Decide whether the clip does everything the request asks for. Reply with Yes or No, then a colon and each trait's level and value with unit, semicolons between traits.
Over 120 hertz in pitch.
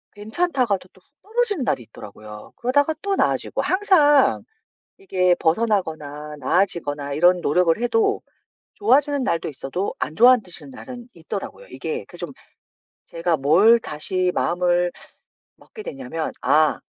Yes: medium, 185 Hz